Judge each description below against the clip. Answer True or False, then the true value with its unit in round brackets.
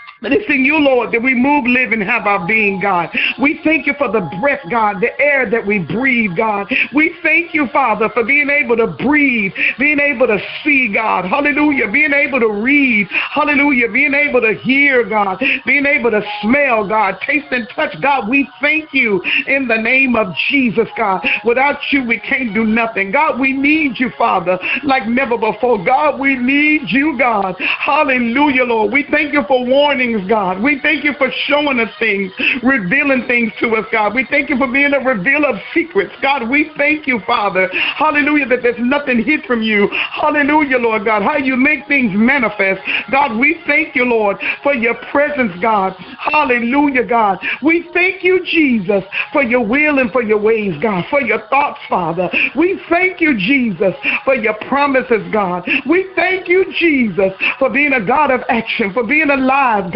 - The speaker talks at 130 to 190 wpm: True (185 wpm)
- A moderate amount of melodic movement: True (4.2 semitones)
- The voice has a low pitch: False (260 Hz)